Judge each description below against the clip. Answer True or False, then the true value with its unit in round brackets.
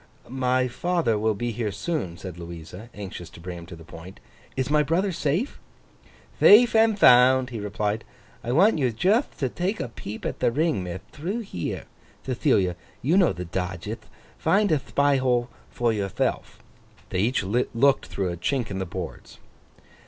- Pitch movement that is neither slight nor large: False (8.0 semitones)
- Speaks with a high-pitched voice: False (120 Hz)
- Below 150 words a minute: False (175 wpm)